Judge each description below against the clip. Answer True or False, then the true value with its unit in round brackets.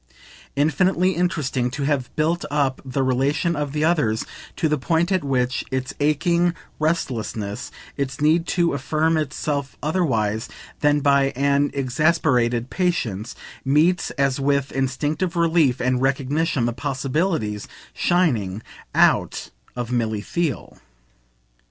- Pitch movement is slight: False (4.1 semitones)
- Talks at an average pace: False (120 wpm)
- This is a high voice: False (140 Hz)